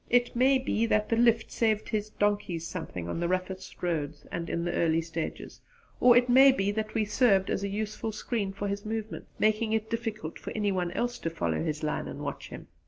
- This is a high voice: Yes, high, 210 Hz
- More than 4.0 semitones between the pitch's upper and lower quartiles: Yes, average, 4.5 semitones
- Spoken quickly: Yes, fast, 220 wpm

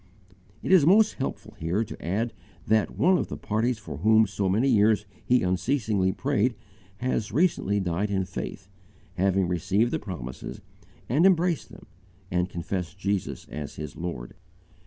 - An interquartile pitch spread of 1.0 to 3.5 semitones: No, average, 5.2 semitones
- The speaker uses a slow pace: No, average, 155 wpm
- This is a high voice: No, low, 100 Hz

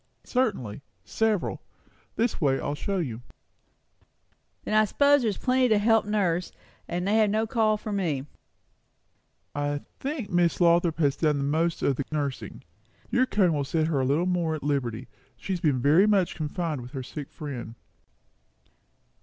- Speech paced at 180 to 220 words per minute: No, average, 170 wpm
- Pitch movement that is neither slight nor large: No, wide, 6.7 semitones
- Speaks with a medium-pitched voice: Yes, medium, 170 Hz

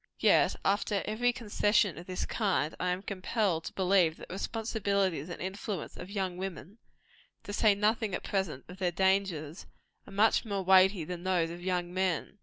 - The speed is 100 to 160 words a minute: No, average, 180 wpm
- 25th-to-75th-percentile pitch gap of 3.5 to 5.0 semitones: No, narrow, 2.4 semitones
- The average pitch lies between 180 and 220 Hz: Yes, high, 190 Hz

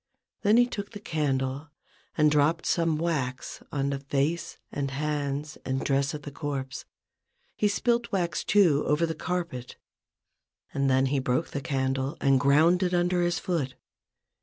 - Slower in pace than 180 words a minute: Yes, average, 160 wpm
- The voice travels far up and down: No, average, 3.8 semitones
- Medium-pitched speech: Yes, medium, 150 Hz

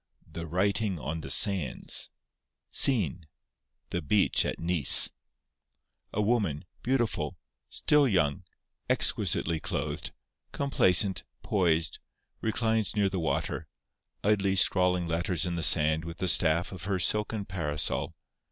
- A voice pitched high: No, very low, 90 Hz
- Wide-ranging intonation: No, average, 4.0 semitones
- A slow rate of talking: Yes, slow, 115 wpm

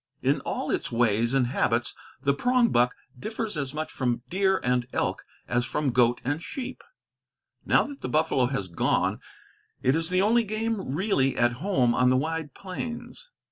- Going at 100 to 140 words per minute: No, average, 170 wpm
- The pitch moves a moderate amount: No, wide, 8.2 semitones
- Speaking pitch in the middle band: Yes, medium, 145 Hz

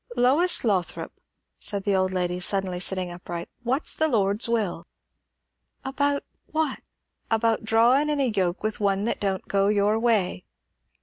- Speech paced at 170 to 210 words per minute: No, average, 145 wpm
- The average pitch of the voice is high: Yes, high, 210 Hz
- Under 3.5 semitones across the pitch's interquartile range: No, average, 4.4 semitones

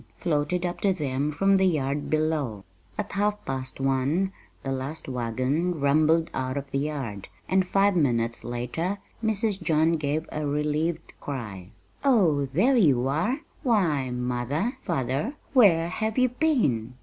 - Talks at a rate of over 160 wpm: No, average, 145 wpm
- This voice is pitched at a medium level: Yes, medium, 150 Hz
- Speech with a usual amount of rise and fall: No, wide, 6.2 semitones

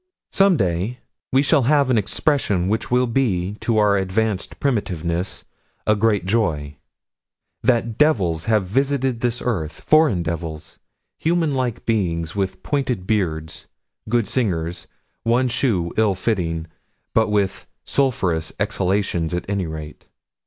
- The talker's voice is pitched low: Yes, low, 105 Hz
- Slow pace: Yes, slow, 130 wpm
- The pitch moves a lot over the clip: Yes, wide, 5.8 semitones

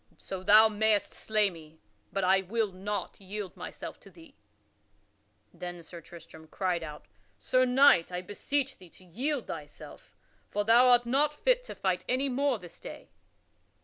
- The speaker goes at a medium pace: Yes, average, 160 wpm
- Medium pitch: No, high, 205 Hz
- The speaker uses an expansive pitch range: Yes, wide, 5.8 semitones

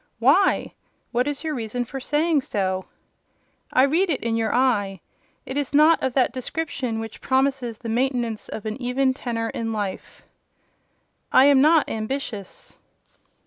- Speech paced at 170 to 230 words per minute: No, average, 150 wpm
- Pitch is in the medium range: No, very high, 250 Hz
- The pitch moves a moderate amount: Yes, average, 3.7 semitones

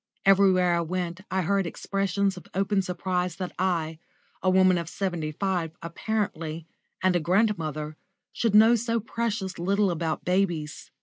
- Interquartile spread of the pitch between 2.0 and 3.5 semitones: Yes, average, 2.7 semitones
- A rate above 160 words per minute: No, average, 145 wpm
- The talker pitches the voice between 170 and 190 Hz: Yes, medium, 185 Hz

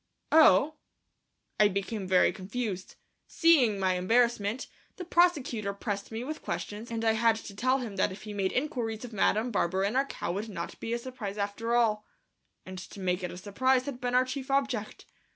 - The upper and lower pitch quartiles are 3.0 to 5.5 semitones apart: Yes, average, 4.0 semitones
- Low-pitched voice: No, high, 220 Hz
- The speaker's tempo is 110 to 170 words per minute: No, average, 190 wpm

